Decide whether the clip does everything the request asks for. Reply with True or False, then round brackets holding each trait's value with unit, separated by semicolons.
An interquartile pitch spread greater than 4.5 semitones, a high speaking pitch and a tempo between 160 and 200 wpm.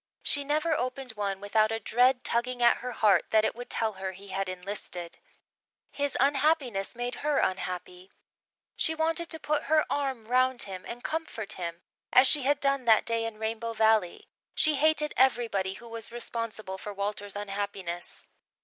True (5.1 semitones; 230 Hz; 170 wpm)